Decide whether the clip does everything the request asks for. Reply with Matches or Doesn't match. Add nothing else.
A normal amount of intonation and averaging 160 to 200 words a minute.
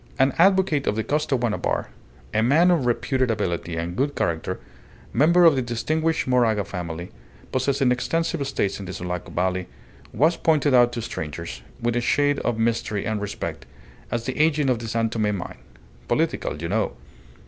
Doesn't match